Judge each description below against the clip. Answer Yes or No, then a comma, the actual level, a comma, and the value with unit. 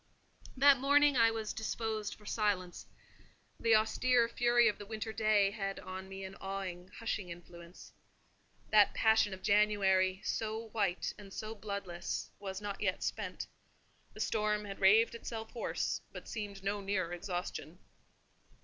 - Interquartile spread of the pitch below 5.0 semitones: Yes, narrow, 2.6 semitones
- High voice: Yes, high, 205 Hz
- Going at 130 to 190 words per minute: Yes, average, 145 wpm